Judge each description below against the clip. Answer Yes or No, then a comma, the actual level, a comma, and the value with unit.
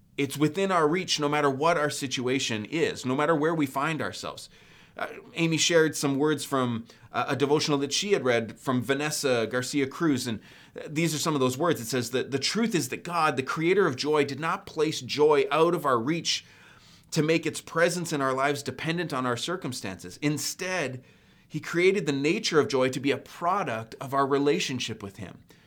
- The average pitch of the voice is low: No, medium, 145 Hz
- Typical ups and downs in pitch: Yes, average, 3.7 semitones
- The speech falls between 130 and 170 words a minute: No, fast, 205 wpm